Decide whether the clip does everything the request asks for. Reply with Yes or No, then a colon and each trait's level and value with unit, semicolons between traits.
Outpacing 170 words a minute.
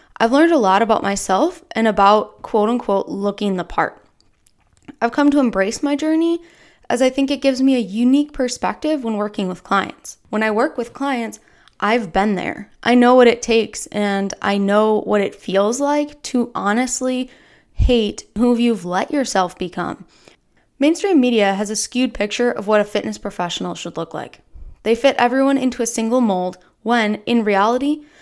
Yes: average, 180 wpm